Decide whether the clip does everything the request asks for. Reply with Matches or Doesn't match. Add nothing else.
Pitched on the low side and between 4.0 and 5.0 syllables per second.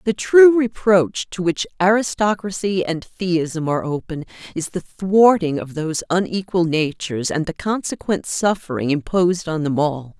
Doesn't match